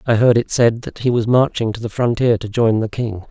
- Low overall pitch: Yes, low, 115 Hz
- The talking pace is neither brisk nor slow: No, fast, 275 wpm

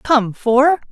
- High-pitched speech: Yes, very high, 260 Hz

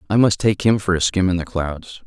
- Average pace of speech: No, fast, 290 wpm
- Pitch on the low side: Yes, very low, 95 Hz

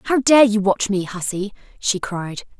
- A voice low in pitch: No, high, 205 Hz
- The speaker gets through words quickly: No, average, 185 wpm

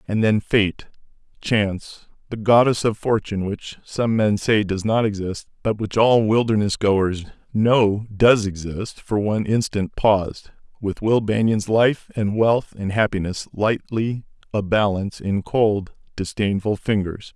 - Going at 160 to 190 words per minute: No, average, 145 wpm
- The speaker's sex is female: No, male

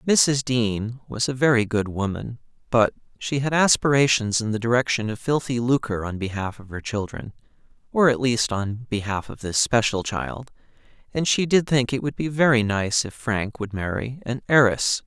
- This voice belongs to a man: Yes, male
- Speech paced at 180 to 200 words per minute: Yes, average, 185 wpm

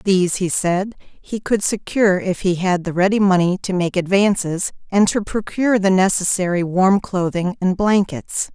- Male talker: No, female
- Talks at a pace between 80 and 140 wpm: No, average, 170 wpm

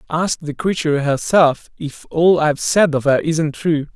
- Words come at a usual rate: Yes, average, 180 wpm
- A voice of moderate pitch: Yes, medium, 155 Hz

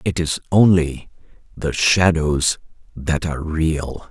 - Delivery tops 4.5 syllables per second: No, 3.6 syllables/s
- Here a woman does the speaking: No, male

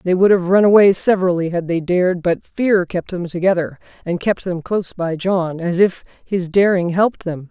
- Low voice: No, medium, 180 Hz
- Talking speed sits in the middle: No, fast, 210 wpm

